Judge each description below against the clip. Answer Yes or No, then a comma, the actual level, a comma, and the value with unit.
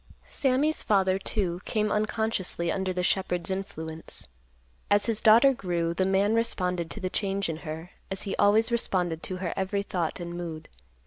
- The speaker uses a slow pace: No, average, 170 wpm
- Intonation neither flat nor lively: Yes, average, 3.3 semitones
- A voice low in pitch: No, high, 190 Hz